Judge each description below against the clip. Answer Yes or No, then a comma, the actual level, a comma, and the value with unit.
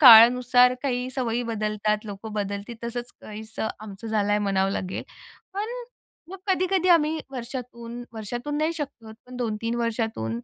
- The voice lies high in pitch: Yes, high, 235 Hz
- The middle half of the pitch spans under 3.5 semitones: Yes, average, 3.1 semitones